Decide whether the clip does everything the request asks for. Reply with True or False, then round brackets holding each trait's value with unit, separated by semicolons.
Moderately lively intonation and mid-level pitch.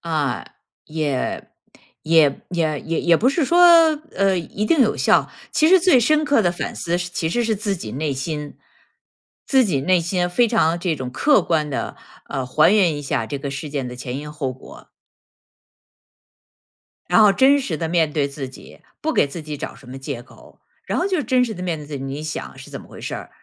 False (6.7 semitones; 165 Hz)